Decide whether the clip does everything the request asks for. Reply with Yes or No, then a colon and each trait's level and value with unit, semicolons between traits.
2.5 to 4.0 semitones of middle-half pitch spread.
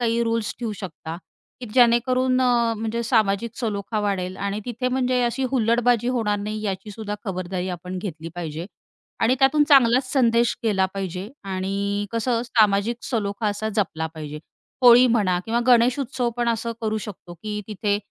Yes: average, 3.4 semitones